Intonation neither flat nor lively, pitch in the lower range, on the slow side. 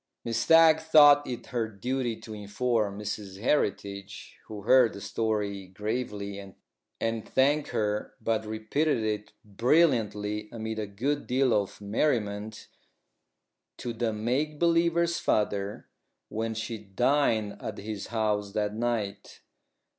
Yes: average, 3.5 semitones; low, 110 Hz; slow, 125 wpm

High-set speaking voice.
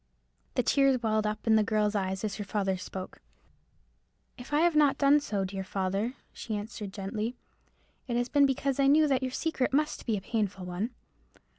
Yes: high, 220 Hz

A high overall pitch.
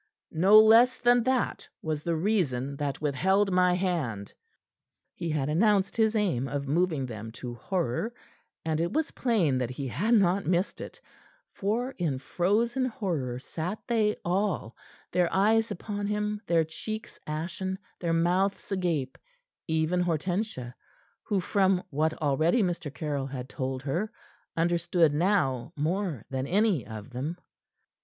No: medium, 175 Hz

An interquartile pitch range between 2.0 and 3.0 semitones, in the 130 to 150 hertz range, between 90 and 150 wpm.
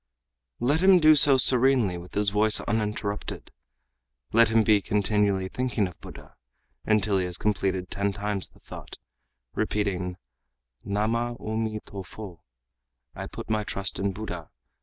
No: narrow, 2.5 semitones; low, 105 Hz; average, 145 wpm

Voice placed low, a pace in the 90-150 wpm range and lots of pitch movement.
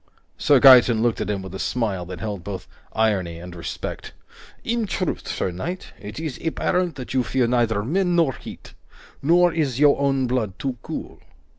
No: low, 125 Hz; average, 180 wpm; wide, 6.8 semitones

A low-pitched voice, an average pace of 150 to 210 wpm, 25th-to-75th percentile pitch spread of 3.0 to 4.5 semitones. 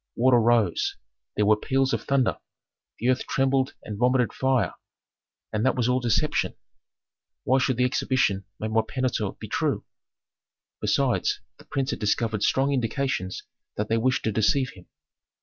Yes: low, 125 Hz; average, 155 wpm; average, 3.3 semitones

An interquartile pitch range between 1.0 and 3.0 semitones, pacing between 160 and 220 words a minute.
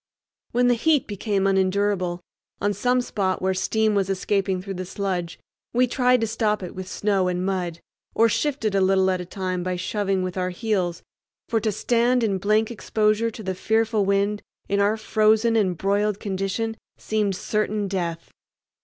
Yes: average, 2.7 semitones; average, 175 wpm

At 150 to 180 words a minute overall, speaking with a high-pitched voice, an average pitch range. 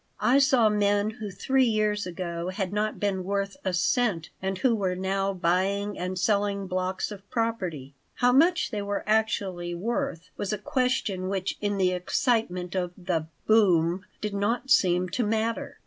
Yes: average, 165 wpm; high, 200 Hz; average, 3.0 semitones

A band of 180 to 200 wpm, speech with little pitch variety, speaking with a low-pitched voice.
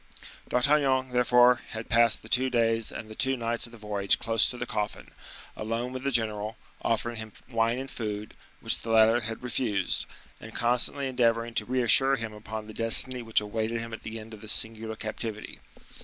Yes: average, 190 wpm; narrow, 2.1 semitones; low, 115 Hz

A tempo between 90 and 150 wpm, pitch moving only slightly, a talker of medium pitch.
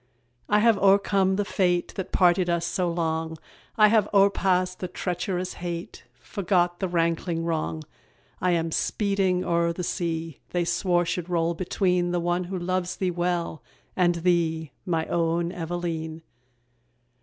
Yes: average, 145 wpm; narrow, 1.7 semitones; medium, 175 Hz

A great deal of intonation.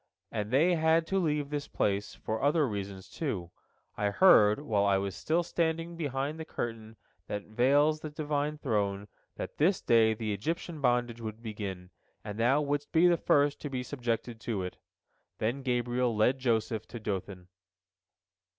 Yes: wide, 5.8 semitones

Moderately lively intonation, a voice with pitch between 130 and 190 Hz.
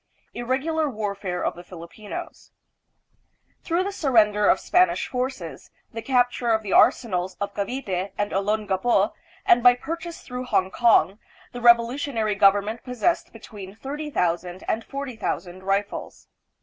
No: average, 4.5 semitones; high, 220 Hz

